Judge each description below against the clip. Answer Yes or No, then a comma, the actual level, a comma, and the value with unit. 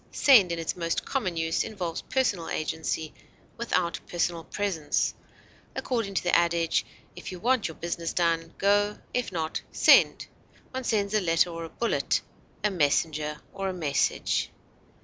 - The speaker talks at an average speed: Yes, average, 150 wpm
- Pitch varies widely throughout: No, average, 3.7 semitones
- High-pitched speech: No, medium, 175 Hz